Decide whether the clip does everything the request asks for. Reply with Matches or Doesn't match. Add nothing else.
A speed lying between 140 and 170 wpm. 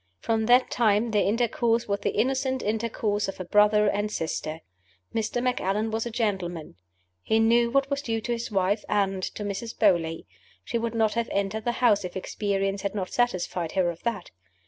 Doesn't match